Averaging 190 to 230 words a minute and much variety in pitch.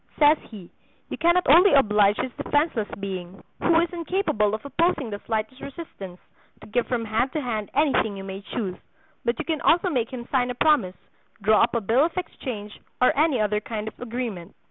Yes: average, 195 wpm; wide, 6.0 semitones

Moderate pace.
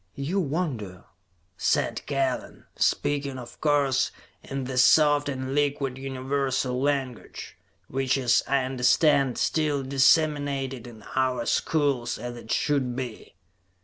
No: slow, 115 wpm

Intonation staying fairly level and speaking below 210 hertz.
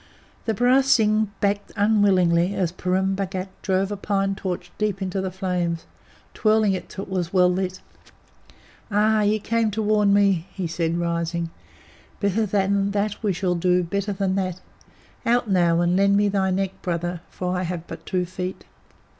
Yes: narrow, 2.2 semitones; high, 190 Hz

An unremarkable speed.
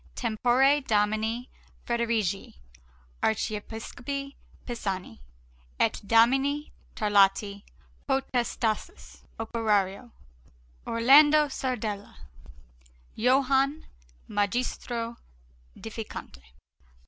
No: slow, 55 wpm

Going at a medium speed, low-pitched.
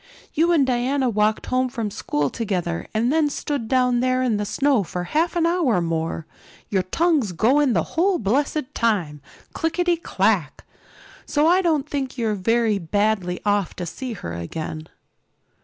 No: average, 160 wpm; high, 235 Hz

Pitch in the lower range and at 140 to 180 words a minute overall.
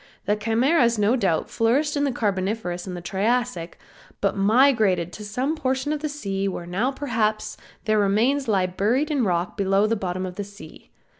No: high, 215 Hz; average, 175 wpm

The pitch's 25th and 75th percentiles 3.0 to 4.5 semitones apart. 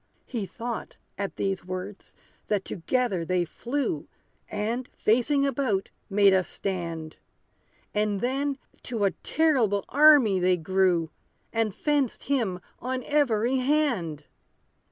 No: wide, 5.6 semitones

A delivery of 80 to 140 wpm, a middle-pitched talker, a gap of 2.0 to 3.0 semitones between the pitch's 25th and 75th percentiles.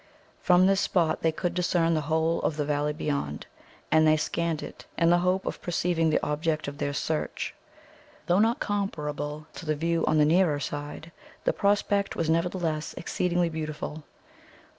No: average, 170 wpm; medium, 160 Hz; narrow, 2.6 semitones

